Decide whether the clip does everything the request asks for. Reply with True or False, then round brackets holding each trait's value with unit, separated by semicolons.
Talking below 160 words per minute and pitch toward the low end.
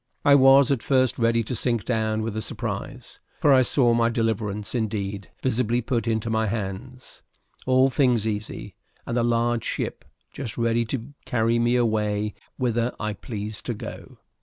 False (165 wpm; 115 Hz)